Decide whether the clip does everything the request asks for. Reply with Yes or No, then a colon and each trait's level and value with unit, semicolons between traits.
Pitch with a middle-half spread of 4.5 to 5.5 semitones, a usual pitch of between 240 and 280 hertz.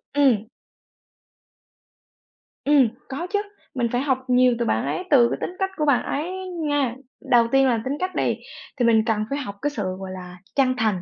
No: average, 3.9 semitones; very high, 255 Hz